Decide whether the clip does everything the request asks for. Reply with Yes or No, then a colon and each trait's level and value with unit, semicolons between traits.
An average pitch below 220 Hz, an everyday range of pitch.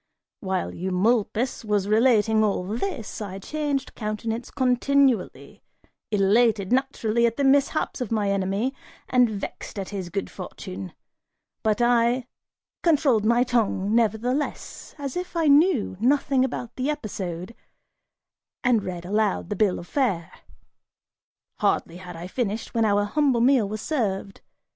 No: high, 225 Hz; average, 4.5 semitones